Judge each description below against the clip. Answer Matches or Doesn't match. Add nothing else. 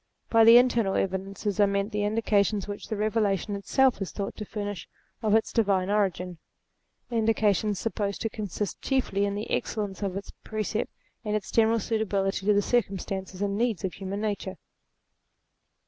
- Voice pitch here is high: Matches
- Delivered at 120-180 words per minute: Matches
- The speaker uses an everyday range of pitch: Doesn't match